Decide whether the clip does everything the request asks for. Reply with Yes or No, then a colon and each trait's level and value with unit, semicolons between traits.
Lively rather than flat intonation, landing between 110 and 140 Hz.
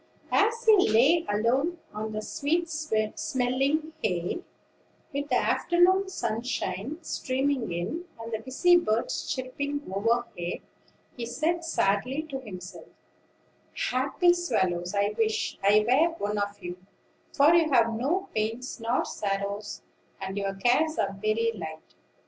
No: wide, 6.9 semitones; high, 240 Hz